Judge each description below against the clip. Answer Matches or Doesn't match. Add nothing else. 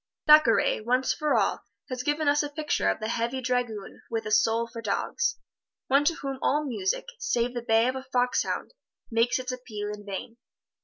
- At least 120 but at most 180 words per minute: Doesn't match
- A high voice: Matches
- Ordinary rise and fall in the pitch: Matches